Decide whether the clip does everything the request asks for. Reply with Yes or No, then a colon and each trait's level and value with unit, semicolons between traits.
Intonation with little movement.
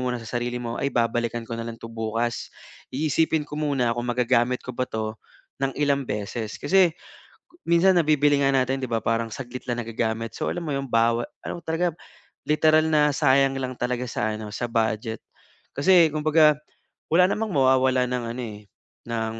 No: average, 4.3 semitones